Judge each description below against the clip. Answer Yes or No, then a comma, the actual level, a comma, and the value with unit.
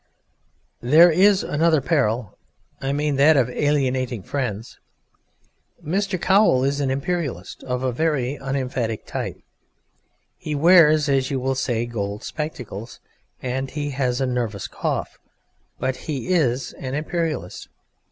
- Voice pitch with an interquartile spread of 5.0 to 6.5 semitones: No, average, 3.5 semitones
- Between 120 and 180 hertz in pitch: Yes, low, 135 Hz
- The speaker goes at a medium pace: No, slow, 125 wpm